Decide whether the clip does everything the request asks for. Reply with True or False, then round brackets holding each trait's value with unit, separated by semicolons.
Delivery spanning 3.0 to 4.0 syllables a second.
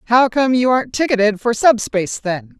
False (5.4 syllables/s)